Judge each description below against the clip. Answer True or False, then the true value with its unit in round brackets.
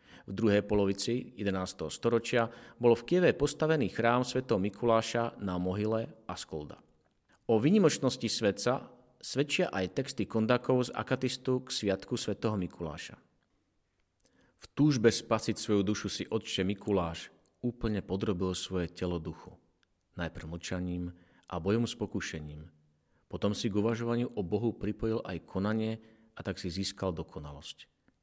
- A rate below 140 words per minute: True (130 wpm)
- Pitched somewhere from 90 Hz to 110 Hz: True (105 Hz)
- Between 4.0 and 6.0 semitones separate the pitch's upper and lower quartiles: True (4.3 semitones)